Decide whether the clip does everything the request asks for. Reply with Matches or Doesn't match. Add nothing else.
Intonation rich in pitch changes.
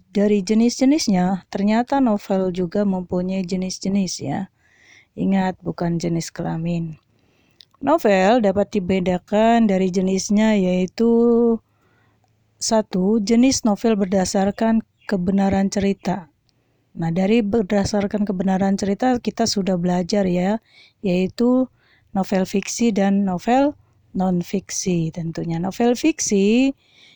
Doesn't match